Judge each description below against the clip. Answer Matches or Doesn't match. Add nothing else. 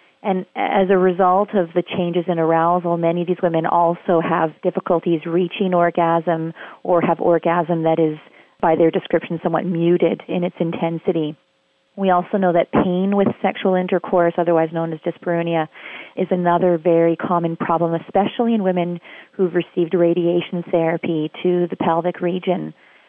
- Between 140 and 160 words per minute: Matches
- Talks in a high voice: Doesn't match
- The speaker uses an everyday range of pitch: Doesn't match